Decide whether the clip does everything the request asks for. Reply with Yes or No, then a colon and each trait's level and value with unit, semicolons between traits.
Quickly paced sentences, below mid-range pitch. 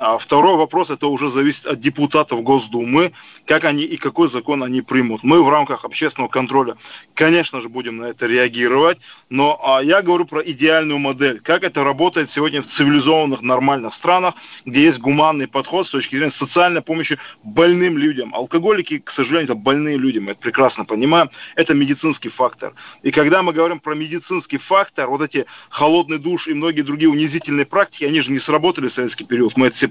No: fast, 185 wpm; medium, 150 Hz